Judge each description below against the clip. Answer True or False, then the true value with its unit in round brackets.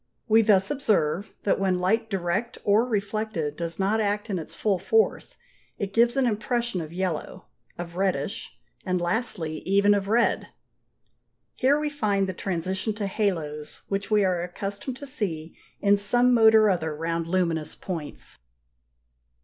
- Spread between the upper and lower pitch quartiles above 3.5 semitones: True (4.0 semitones)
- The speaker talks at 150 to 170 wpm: True (155 wpm)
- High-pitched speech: True (195 Hz)